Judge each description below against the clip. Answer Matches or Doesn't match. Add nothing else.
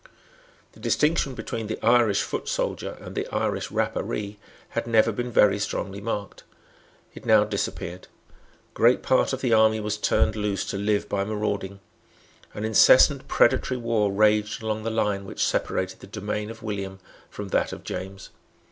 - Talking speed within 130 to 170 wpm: Matches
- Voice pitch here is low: Matches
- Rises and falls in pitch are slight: Matches